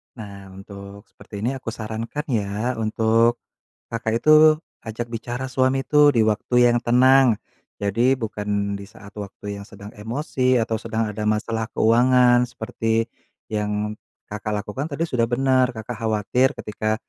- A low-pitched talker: Yes, low, 115 Hz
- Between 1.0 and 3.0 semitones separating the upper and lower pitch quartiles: Yes, average, 2.7 semitones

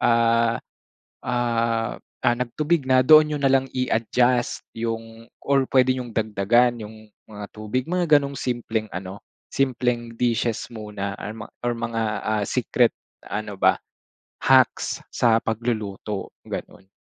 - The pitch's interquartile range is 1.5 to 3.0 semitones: Yes, narrow, 2.6 semitones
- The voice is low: Yes, low, 115 Hz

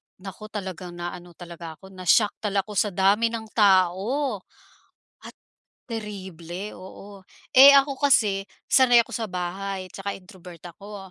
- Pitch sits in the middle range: No, high, 195 Hz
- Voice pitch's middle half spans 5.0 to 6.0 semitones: No, average, 2.8 semitones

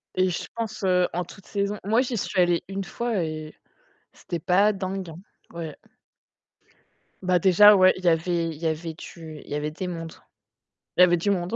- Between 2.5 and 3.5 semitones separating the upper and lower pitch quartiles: Yes, average, 3.0 semitones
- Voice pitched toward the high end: No, medium, 180 Hz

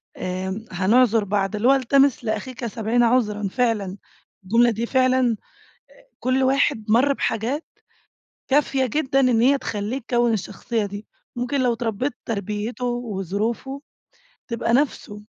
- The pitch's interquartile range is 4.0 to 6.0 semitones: No, average, 3.5 semitones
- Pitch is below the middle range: No, high, 235 Hz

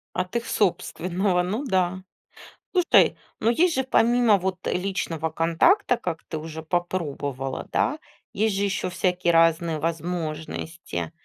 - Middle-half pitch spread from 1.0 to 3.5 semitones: No, average, 4.0 semitones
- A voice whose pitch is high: No, medium, 180 Hz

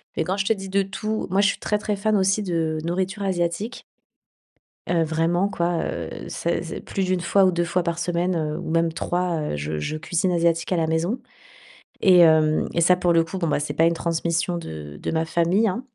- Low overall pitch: No, medium, 175 Hz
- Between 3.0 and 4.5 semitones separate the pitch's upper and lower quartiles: No, narrow, 2.6 semitones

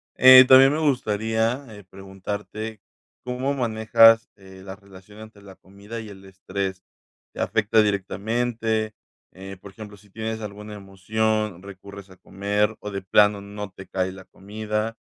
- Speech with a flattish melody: Yes, narrow, 2.3 semitones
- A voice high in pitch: No, low, 105 Hz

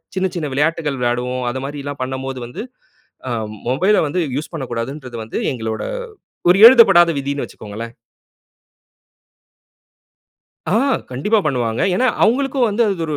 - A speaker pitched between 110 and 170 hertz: Yes, medium, 140 Hz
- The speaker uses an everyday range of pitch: No, wide, 6.4 semitones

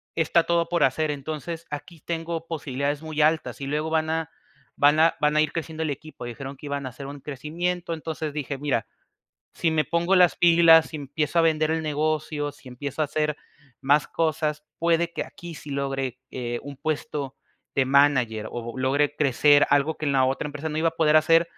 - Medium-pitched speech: Yes, medium, 150 Hz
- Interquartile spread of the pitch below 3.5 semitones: Yes, narrow, 2.4 semitones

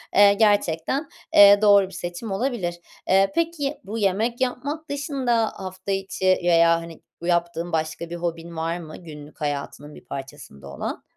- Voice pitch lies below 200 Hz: Yes, medium, 185 Hz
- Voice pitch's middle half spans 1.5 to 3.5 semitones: No, average, 5.0 semitones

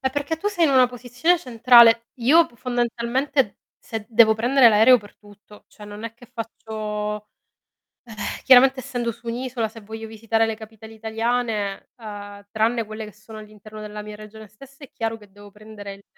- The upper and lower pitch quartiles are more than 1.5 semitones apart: Yes, narrow, 2.6 semitones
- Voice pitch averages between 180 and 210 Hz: No, high, 225 Hz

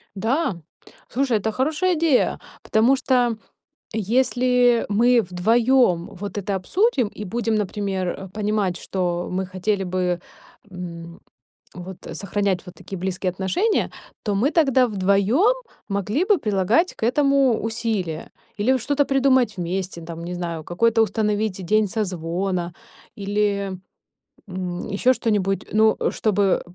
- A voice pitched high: Yes, high, 205 Hz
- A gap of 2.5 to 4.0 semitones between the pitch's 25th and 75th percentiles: No, average, 4.7 semitones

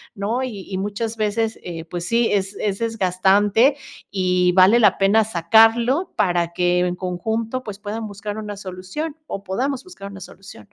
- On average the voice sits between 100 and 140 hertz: No, high, 205 Hz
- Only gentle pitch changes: No, average, 3.4 semitones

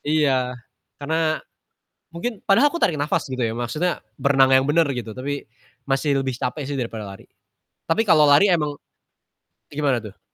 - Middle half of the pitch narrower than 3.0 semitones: No, average, 3.7 semitones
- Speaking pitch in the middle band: Yes, medium, 145 Hz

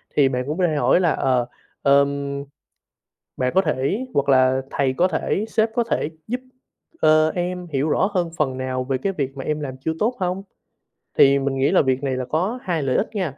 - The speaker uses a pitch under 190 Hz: Yes, medium, 140 Hz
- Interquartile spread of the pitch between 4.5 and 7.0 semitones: Yes, average, 5.2 semitones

